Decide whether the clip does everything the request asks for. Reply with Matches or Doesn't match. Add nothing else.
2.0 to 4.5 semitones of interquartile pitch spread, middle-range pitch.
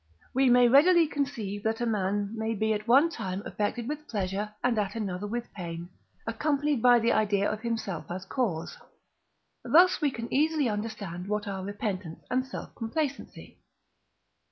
Doesn't match